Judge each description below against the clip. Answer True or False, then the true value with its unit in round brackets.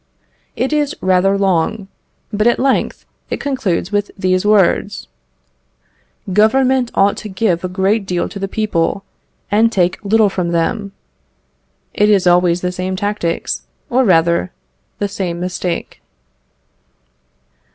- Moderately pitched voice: False (195 Hz)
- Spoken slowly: True (130 wpm)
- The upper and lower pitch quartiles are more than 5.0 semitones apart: False (2.9 semitones)